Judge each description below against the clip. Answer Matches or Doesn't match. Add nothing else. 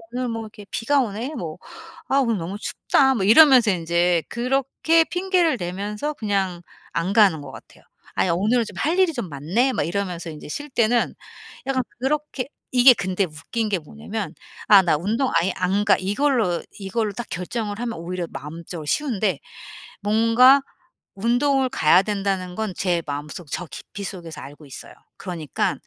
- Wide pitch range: Matches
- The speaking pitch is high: Matches